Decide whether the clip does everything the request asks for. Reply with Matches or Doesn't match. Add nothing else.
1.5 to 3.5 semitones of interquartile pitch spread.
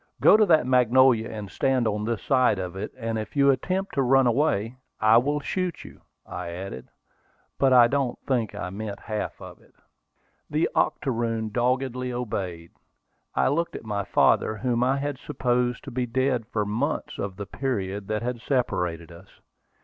Doesn't match